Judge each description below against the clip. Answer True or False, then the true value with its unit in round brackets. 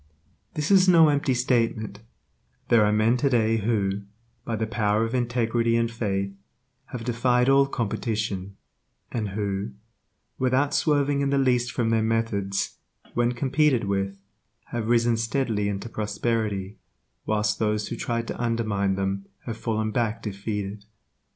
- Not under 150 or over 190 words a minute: False (140 wpm)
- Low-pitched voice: True (115 Hz)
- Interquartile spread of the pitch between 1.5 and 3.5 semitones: True (2.8 semitones)